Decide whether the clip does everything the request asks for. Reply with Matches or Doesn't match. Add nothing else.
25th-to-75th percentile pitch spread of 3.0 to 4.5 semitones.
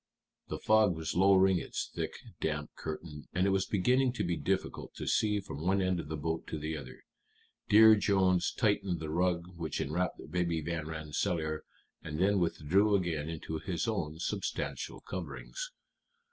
Matches